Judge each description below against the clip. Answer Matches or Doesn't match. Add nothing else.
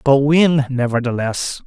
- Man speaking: Matches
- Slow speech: Matches